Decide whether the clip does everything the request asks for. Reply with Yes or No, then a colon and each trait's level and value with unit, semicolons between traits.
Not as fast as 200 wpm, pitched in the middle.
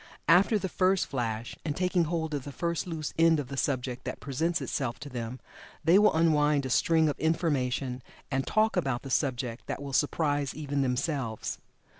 Yes: average, 185 wpm; medium, 145 Hz